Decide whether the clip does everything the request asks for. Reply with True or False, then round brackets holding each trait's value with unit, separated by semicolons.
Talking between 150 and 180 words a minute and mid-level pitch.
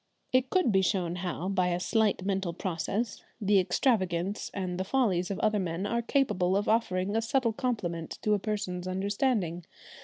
False (175 wpm; 195 Hz)